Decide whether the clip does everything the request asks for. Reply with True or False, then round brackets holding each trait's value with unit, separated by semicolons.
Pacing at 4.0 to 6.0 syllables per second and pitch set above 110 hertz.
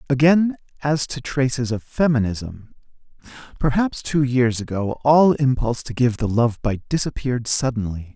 True (4.7 syllables/s; 125 Hz)